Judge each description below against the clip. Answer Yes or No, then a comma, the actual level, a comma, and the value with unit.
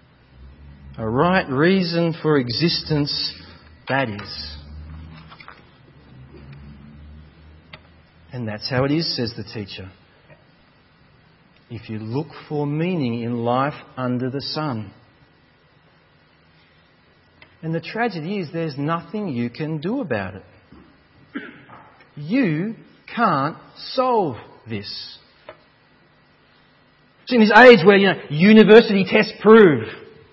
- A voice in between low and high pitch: No, low, 130 Hz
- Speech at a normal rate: No, slow, 100 wpm